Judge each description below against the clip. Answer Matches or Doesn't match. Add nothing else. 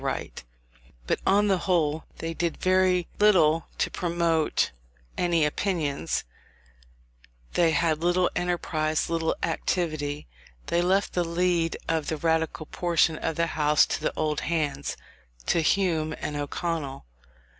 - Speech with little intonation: Matches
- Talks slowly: Matches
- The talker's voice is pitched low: Doesn't match